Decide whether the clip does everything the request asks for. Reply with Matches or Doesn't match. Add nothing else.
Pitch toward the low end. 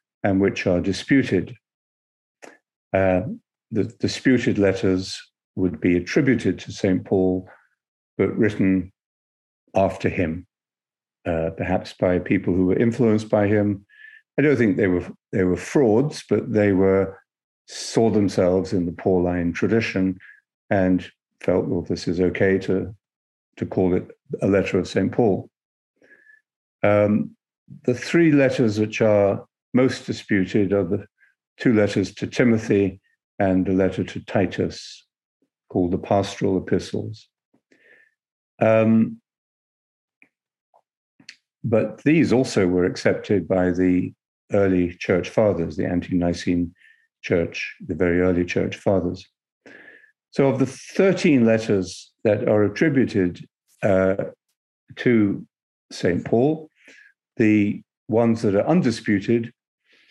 Matches